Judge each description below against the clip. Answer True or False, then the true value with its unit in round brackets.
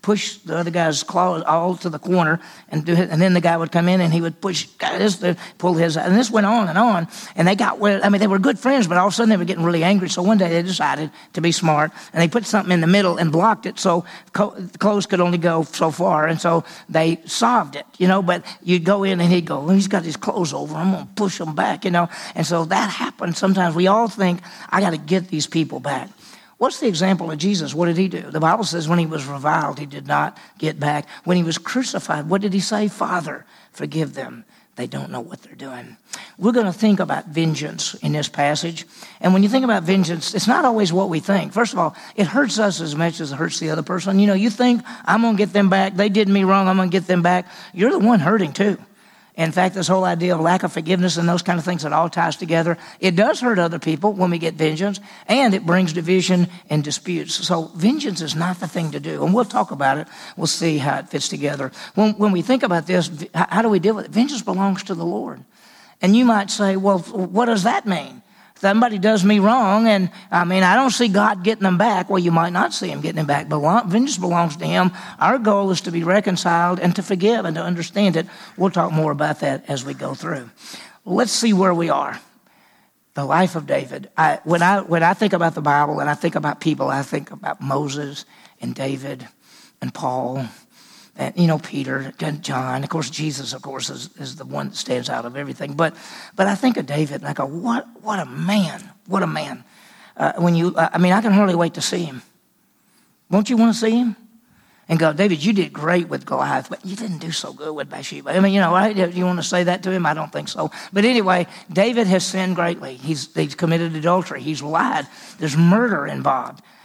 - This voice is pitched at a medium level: True (180 Hz)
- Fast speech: True (245 wpm)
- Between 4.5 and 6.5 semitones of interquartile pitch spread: False (3.7 semitones)